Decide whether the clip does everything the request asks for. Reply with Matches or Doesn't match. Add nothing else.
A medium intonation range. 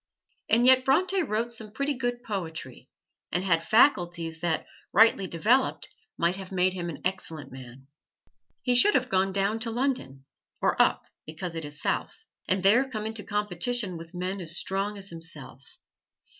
Doesn't match